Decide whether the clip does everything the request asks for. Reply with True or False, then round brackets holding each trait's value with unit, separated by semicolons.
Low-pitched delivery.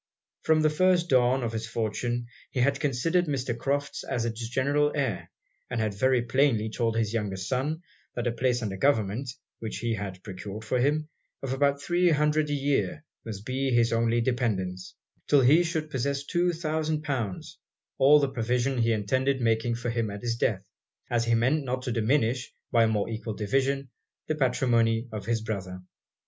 True (120 Hz)